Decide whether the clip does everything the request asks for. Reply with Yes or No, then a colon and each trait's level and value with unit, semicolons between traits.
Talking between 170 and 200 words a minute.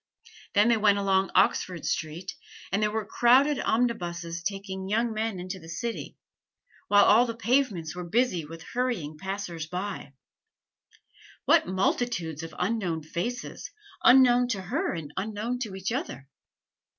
No: average, 140 wpm